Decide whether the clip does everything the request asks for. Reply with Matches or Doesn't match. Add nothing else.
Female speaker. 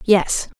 Matches